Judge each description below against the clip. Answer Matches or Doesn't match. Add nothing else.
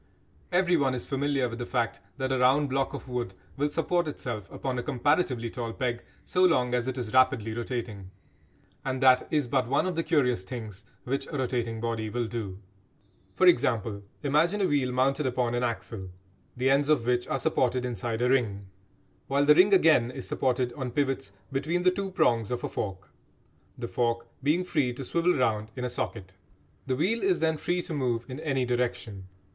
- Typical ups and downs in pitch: Matches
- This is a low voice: Matches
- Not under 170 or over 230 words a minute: Matches